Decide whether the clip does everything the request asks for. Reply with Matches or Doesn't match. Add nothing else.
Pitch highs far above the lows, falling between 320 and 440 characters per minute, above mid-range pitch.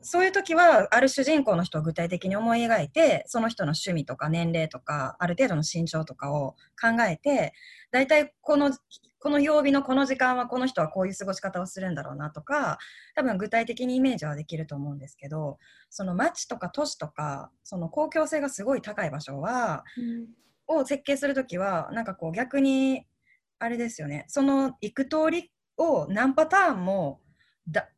Matches